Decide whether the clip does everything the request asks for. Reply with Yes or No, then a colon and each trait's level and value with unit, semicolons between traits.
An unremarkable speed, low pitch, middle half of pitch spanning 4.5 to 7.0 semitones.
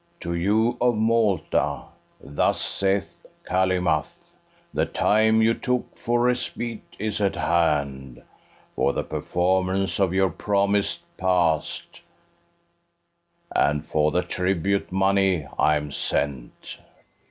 No: slow, 105 wpm; very low, 95 Hz; average, 4.8 semitones